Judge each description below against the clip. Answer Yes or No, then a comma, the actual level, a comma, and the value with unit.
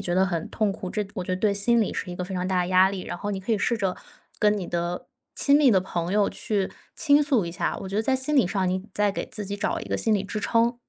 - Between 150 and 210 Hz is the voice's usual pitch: Yes, high, 200 Hz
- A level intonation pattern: No, average, 3.0 semitones